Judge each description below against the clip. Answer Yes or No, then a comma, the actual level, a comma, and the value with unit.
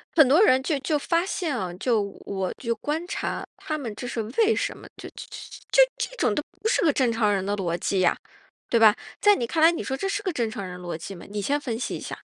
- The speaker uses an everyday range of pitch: No, wide, 8.0 semitones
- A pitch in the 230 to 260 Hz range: Yes, very high, 250 Hz